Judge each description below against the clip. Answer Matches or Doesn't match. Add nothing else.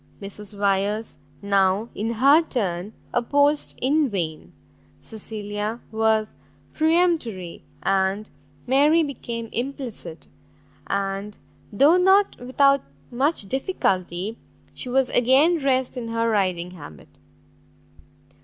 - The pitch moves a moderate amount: Doesn't match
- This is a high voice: Matches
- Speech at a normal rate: Doesn't match